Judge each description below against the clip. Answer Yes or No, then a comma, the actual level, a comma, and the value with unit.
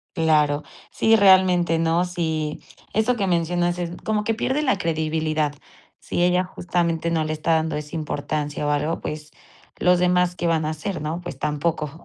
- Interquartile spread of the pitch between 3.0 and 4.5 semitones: No, narrow, 2.5 semitones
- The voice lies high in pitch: No, medium, 165 Hz